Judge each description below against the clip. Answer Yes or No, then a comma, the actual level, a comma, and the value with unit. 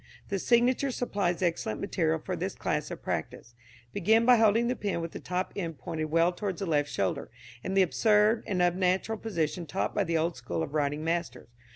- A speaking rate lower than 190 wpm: No, average, 200 wpm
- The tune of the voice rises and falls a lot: No, average, 4.5 semitones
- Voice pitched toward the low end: No, medium, 180 Hz